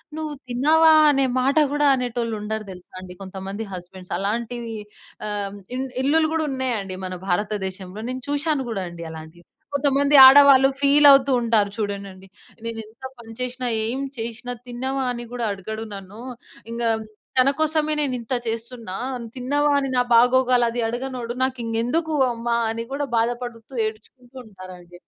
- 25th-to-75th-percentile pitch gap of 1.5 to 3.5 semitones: No, average, 4.1 semitones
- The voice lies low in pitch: No, high, 235 Hz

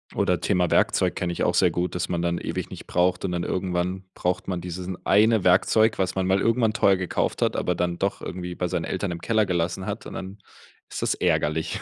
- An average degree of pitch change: No, narrow, 1.5 semitones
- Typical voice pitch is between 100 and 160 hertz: No, very low, 90 Hz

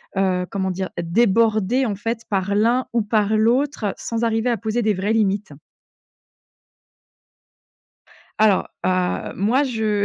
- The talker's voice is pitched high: Yes, high, 215 Hz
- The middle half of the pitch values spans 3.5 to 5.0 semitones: No, average, 2.9 semitones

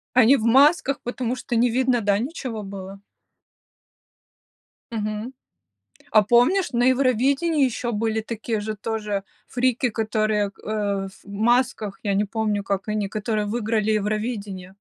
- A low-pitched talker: No, high, 220 Hz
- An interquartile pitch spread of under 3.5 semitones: Yes, average, 2.9 semitones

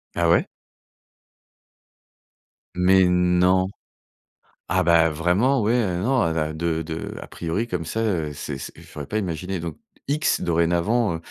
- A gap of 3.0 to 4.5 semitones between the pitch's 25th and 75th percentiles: Yes, average, 3.3 semitones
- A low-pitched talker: Yes, very low, 90 Hz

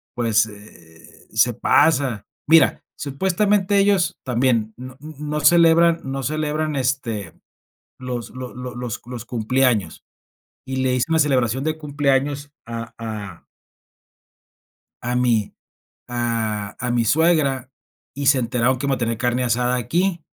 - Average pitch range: Yes, average, 4.2 semitones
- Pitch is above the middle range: No, low, 125 Hz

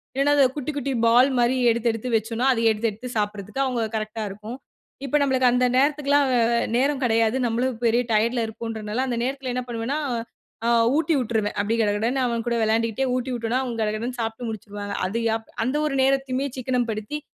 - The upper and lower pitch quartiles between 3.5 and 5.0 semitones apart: No, average, 2.8 semitones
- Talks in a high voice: Yes, high, 235 Hz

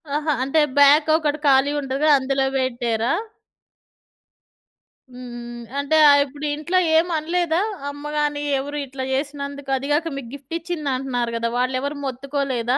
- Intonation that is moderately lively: No, narrow, 2.2 semitones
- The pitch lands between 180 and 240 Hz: No, very high, 280 Hz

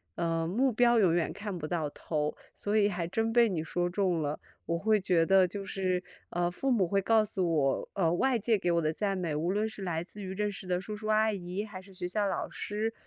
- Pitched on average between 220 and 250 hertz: No, high, 190 Hz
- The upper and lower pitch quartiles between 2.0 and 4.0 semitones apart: Yes, average, 3.5 semitones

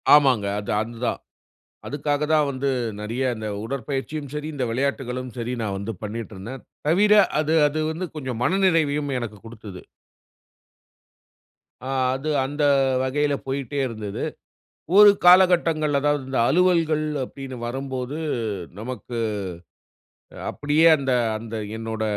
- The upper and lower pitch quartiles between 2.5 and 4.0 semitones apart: No, average, 4.4 semitones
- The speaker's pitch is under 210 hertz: Yes, low, 135 Hz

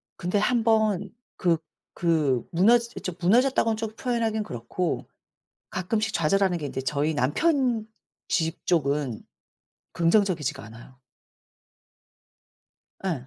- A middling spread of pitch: No, wide, 6.7 semitones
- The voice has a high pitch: No, medium, 180 Hz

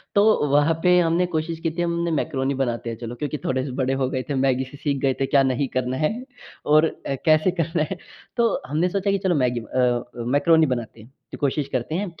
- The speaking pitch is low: No, medium, 145 Hz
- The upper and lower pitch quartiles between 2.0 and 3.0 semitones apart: No, average, 4.5 semitones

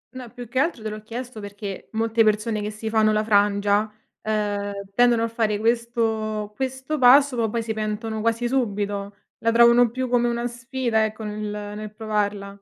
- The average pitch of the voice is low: No, high, 220 Hz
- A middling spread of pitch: No, narrow, 2.2 semitones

